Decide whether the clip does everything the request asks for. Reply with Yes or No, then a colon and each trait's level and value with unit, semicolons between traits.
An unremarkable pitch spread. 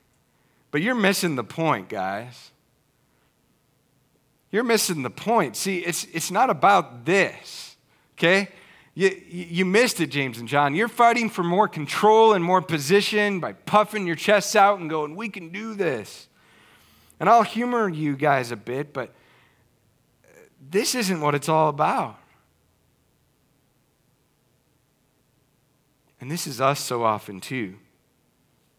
No: wide, 6.0 semitones